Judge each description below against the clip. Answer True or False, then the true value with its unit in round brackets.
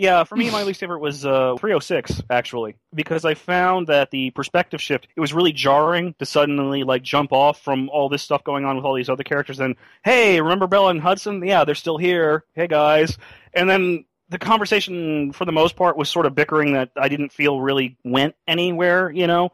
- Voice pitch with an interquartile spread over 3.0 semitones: True (4.3 semitones)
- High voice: False (150 Hz)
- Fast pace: True (210 wpm)